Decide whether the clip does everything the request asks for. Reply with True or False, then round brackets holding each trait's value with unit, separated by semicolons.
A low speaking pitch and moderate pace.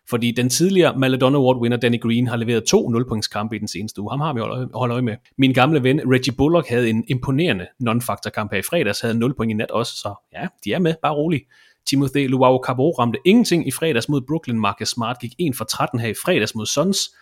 False (125 Hz; 240 wpm)